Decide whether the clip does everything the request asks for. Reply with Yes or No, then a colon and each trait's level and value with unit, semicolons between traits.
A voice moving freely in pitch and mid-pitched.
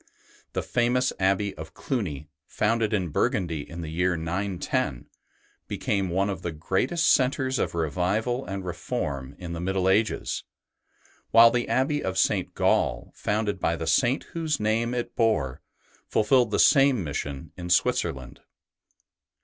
No: wide, 5.9 semitones; very low, 95 Hz